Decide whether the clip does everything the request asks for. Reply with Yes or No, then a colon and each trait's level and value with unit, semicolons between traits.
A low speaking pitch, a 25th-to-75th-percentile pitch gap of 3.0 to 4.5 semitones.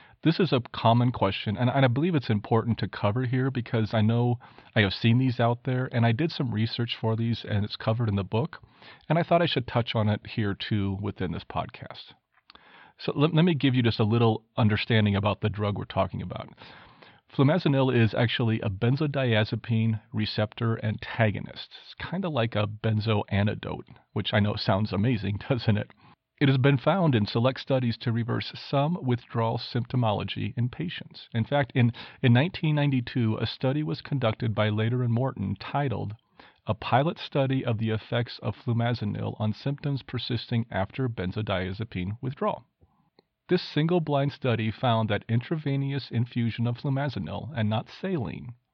Yes: low, 115 Hz; average, 3.7 semitones